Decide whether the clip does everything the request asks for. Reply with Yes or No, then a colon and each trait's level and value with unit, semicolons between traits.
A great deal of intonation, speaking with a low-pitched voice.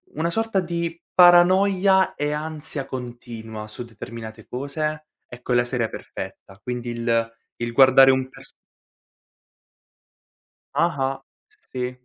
Yes: wide, 5.9 semitones; low, 130 Hz